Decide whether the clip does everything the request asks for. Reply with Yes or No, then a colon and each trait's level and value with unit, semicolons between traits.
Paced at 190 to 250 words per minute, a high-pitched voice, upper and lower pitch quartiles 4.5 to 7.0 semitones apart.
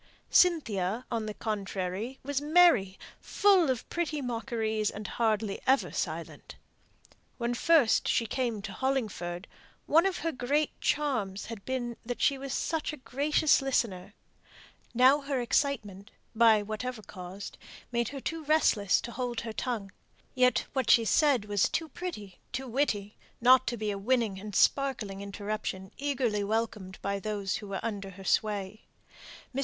No: average, 150 wpm; high, 230 Hz; average, 4.8 semitones